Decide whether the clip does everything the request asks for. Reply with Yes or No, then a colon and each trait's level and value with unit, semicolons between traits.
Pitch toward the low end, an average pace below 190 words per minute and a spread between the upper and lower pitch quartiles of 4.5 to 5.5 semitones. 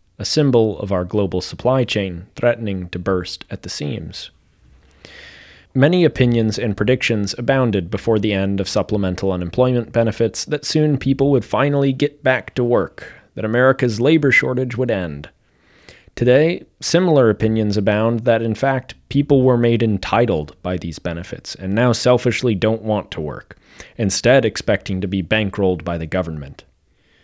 Yes: low, 110 Hz; average, 150 wpm; average, 4.9 semitones